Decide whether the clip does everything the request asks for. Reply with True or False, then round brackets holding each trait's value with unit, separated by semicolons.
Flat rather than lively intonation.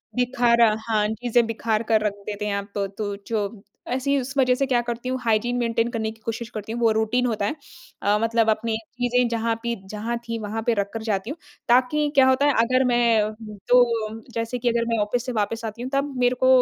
True (2.2 semitones)